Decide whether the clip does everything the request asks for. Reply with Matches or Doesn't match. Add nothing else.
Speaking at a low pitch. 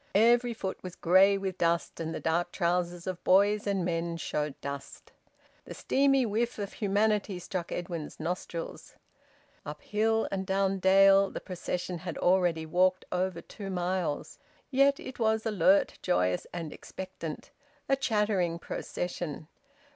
Doesn't match